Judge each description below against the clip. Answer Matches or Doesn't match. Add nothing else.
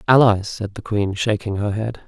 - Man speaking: Matches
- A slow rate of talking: Doesn't match